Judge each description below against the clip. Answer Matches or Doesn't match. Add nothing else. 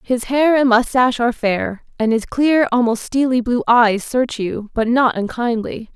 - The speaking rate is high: Doesn't match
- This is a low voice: Doesn't match